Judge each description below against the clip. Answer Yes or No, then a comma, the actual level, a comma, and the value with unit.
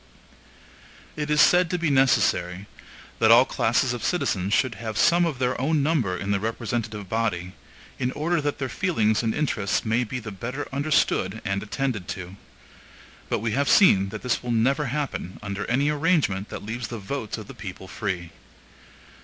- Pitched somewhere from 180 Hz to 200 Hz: No, low, 120 Hz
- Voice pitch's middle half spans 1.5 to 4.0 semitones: No, wide, 5.6 semitones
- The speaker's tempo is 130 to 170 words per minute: No, average, 180 wpm